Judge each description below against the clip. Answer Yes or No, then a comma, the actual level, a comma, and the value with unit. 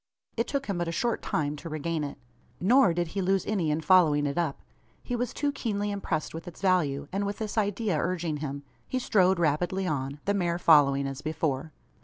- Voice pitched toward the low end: No, medium, 175 Hz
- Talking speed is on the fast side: Yes, fast, 210 wpm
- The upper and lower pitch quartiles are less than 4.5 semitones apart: No, average, 5.0 semitones